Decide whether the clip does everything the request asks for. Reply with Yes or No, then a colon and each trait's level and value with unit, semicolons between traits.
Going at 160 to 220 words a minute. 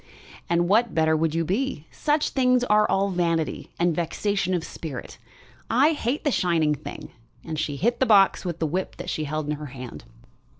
Yes: average, 185 wpm